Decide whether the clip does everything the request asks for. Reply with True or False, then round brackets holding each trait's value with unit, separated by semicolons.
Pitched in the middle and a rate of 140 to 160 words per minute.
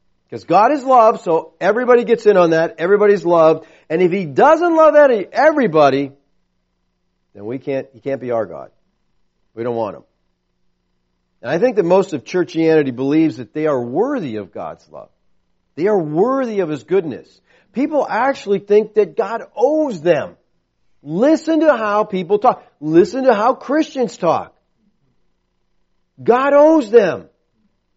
True (180 Hz; 150 wpm)